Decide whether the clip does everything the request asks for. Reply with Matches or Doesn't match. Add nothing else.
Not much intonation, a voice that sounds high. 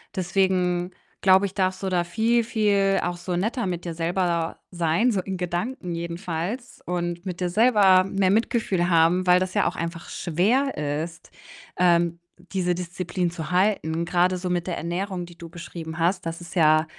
Doesn't match